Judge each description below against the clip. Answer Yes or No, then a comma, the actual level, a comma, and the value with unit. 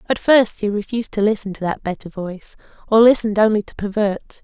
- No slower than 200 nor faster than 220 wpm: Yes, fast, 205 wpm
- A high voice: Yes, high, 210 Hz